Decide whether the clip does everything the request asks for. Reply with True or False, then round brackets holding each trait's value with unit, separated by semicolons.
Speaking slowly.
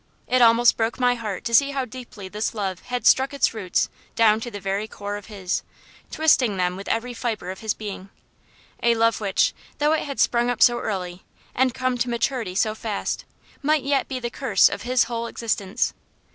False (200 wpm)